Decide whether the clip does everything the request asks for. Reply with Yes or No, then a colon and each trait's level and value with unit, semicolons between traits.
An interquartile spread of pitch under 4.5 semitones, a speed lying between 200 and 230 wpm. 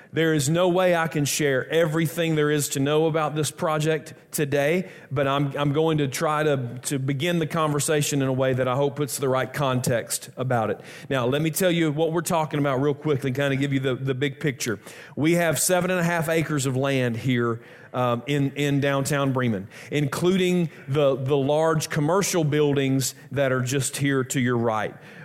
Yes: average, 2.8 semitones; fast, 205 wpm